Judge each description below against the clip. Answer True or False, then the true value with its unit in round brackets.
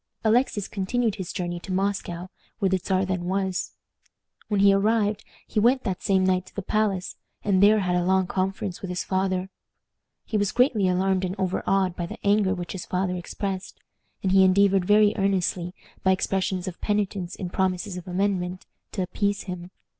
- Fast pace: False (180 wpm)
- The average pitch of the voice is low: False (190 Hz)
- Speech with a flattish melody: True (1.7 semitones)